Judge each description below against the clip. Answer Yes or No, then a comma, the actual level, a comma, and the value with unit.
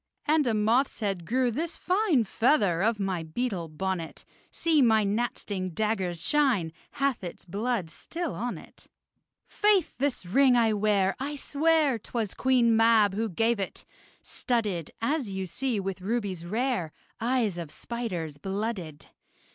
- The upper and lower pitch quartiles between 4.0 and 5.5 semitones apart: Yes, average, 5.1 semitones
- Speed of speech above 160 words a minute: No, average, 145 wpm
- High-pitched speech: Yes, high, 220 Hz